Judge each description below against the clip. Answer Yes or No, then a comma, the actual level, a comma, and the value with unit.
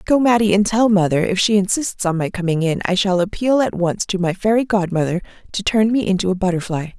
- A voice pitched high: Yes, high, 195 Hz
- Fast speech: Yes, fast, 230 wpm